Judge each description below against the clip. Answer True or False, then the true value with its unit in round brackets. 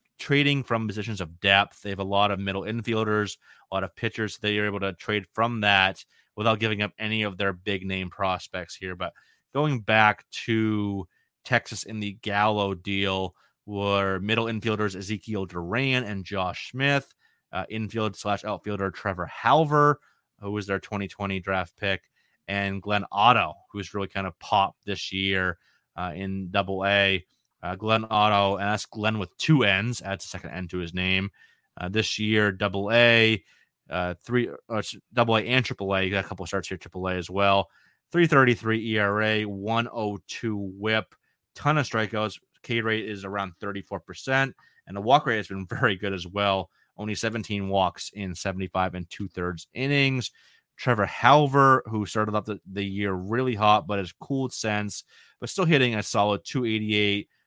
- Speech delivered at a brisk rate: False (170 wpm)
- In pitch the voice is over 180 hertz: False (105 Hz)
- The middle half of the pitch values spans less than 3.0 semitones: True (2.4 semitones)